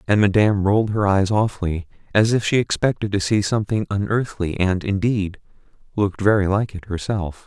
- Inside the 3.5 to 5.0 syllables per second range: No, 5.6 syllables/s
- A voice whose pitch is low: Yes, low, 100 Hz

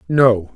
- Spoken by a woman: No, male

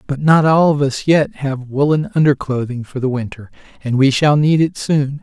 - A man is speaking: Yes, male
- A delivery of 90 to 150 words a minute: No, fast, 205 wpm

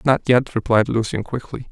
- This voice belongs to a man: Yes, male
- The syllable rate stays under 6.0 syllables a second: Yes, 5.2 syllables/s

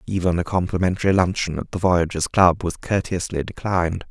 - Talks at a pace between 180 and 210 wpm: No, average, 160 wpm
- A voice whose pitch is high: No, very low, 90 Hz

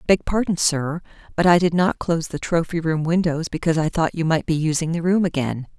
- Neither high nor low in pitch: Yes, medium, 165 Hz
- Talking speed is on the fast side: Yes, fast, 230 wpm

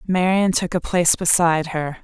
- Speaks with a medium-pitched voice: Yes, medium, 175 Hz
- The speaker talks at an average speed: Yes, average, 175 wpm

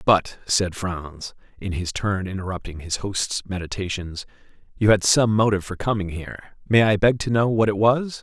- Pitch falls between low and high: No, low, 100 Hz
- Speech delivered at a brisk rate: No, average, 180 wpm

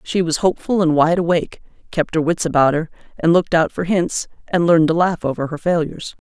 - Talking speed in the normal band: No, fast, 220 wpm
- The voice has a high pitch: No, medium, 165 Hz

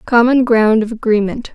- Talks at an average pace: Yes, average, 155 wpm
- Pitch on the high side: Yes, high, 230 Hz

